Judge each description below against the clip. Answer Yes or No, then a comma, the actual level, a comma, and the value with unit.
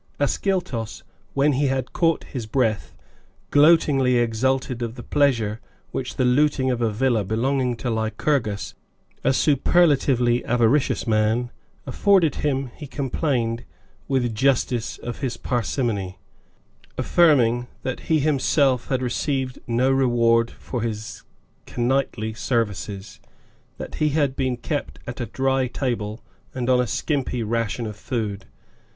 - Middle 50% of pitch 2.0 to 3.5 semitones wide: Yes, average, 3.0 semitones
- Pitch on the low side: Yes, low, 125 Hz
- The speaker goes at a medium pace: No, slow, 130 wpm